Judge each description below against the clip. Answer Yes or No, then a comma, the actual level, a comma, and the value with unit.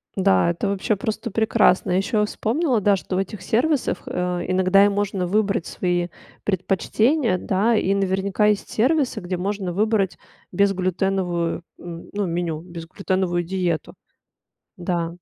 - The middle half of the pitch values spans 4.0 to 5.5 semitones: No, average, 2.8 semitones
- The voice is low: No, high, 190 Hz